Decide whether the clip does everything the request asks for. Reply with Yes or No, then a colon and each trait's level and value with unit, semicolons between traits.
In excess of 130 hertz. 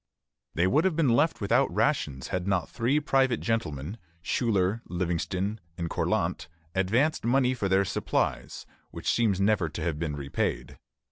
No: low, 100 Hz